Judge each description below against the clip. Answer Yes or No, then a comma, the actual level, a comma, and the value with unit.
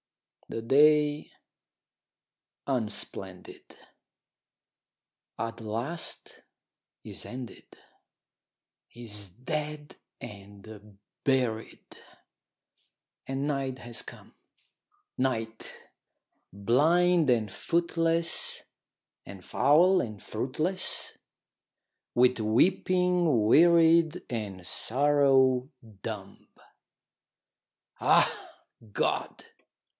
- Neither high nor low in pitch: No, low, 130 Hz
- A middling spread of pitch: No, wide, 5.8 semitones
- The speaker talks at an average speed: No, slow, 60 wpm